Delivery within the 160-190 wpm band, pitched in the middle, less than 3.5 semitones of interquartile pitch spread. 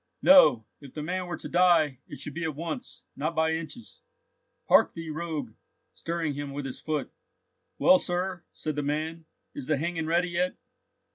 Yes: average, 180 wpm; medium, 160 Hz; average, 2.8 semitones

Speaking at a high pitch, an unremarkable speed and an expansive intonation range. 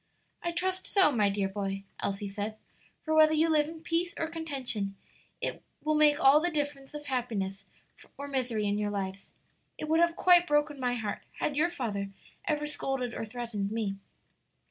Yes: very high, 270 Hz; average, 175 wpm; wide, 7.0 semitones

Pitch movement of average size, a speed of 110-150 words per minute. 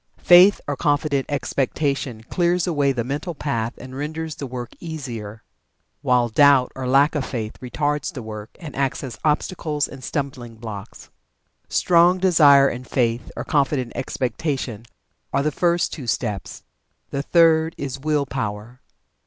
Yes: average, 3.8 semitones; average, 145 wpm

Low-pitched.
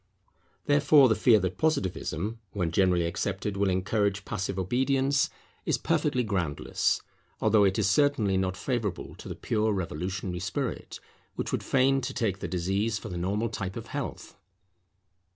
Yes: low, 100 Hz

